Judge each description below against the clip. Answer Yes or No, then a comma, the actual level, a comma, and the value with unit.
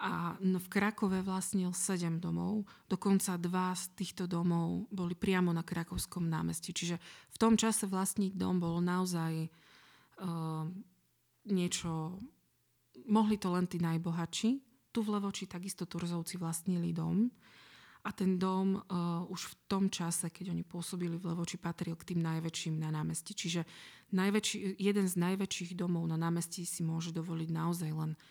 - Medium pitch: Yes, medium, 180 Hz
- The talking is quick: No, average, 150 wpm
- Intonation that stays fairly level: Yes, narrow, 2.3 semitones